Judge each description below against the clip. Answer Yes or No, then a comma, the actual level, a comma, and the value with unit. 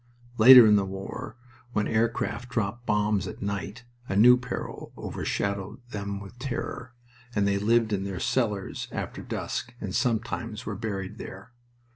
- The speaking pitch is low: Yes, low, 105 Hz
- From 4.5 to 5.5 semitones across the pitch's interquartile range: No, average, 2.9 semitones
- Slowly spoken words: No, average, 155 wpm